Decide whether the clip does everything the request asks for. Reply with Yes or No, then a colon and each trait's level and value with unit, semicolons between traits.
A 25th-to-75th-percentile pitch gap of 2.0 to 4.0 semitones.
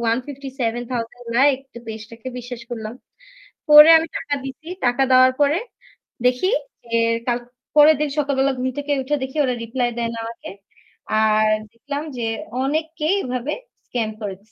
Yes: average, 3.6 semitones